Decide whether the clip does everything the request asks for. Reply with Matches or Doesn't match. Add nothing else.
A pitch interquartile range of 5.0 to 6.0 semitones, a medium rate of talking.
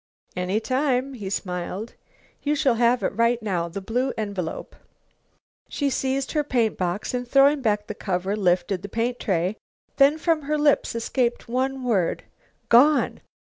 Matches